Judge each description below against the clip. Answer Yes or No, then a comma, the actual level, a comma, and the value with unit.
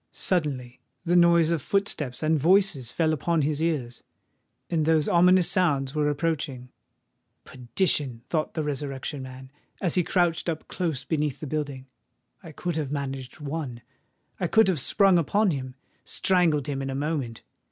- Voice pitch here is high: No, medium, 150 Hz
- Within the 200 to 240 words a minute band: No, average, 150 wpm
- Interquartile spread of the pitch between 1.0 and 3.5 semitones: No, average, 4.0 semitones